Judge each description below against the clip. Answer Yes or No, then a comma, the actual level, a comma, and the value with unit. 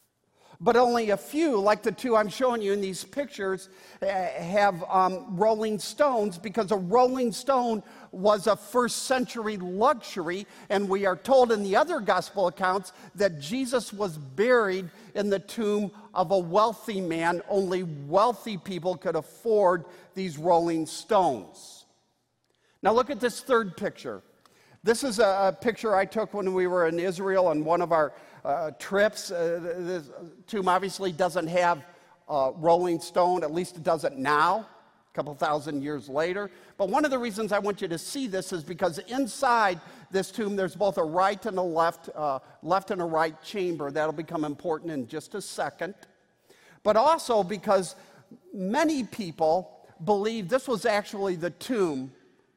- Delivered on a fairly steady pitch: No, average, 3.7 semitones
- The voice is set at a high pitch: Yes, high, 195 Hz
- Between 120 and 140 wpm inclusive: No, average, 165 wpm